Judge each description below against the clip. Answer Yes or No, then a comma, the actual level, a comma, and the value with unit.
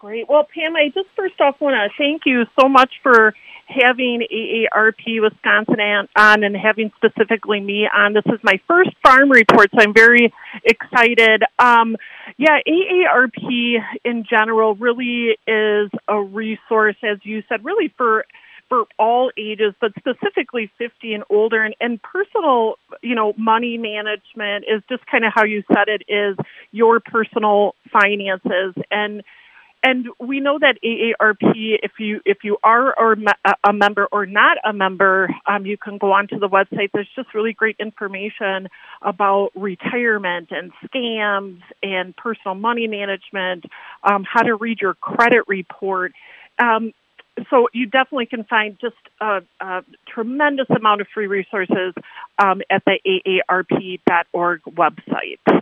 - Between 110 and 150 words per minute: Yes, average, 145 wpm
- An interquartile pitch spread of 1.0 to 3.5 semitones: Yes, average, 2.8 semitones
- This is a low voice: No, high, 220 Hz